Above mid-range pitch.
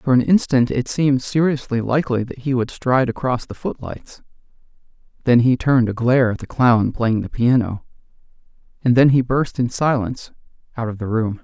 No: low, 125 Hz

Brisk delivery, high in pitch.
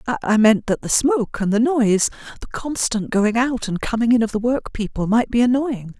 Yes: fast, 210 wpm; high, 230 Hz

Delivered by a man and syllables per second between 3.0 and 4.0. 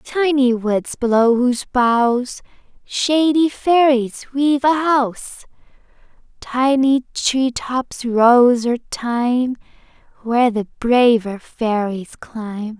No: female; 3.2 syllables/s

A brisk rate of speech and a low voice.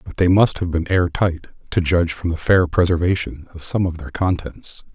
Yes: fast, 220 wpm; very low, 85 Hz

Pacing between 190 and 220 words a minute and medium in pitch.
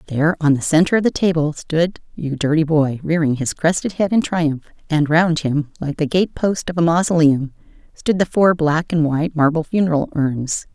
Yes: average, 200 wpm; medium, 160 Hz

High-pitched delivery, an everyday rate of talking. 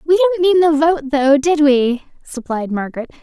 Yes: very high, 295 Hz; average, 185 wpm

